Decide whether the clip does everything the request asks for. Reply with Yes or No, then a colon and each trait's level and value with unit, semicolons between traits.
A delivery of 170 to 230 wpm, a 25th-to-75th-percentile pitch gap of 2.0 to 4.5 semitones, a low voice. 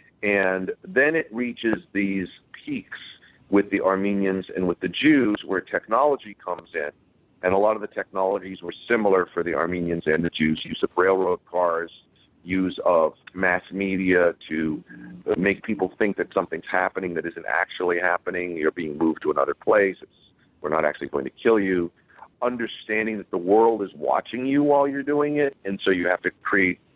Yes: average, 180 wpm; average, 3.7 semitones; very low, 95 Hz